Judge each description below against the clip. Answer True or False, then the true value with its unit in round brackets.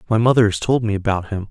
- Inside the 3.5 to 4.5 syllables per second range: False (6.9 syllables/s)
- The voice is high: False (110 Hz)